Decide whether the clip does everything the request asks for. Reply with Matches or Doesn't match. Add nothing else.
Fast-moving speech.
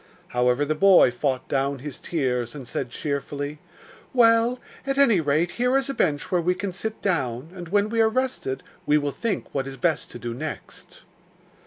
Doesn't match